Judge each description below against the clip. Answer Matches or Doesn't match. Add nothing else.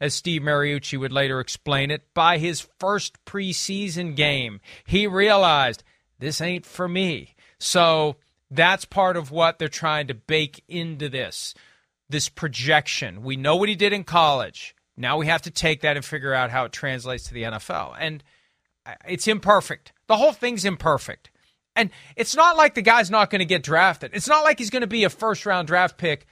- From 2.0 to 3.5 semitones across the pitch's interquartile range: Doesn't match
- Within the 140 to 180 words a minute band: Doesn't match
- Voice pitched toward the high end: Doesn't match